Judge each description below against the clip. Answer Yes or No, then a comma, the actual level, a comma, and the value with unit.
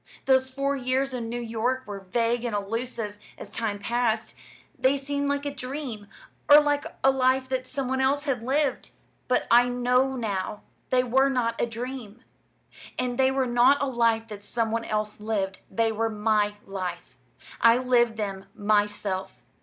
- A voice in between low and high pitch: No, high, 240 Hz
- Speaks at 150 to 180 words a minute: Yes, average, 170 wpm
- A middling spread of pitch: Yes, average, 3.3 semitones